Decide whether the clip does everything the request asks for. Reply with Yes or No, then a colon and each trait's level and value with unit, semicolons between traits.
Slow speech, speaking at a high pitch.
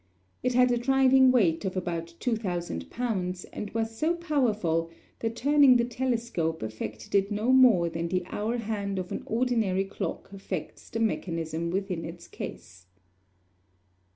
No: average, 150 wpm; high, 205 Hz